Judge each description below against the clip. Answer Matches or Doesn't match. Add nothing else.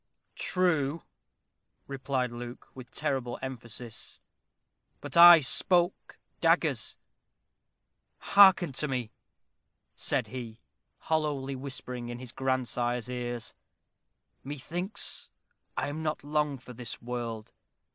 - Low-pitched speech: Matches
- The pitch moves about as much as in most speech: Matches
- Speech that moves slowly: Matches